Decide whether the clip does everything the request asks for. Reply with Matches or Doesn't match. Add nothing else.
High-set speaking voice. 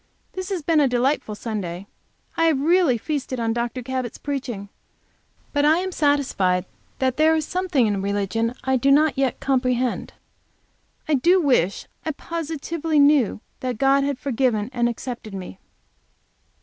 Matches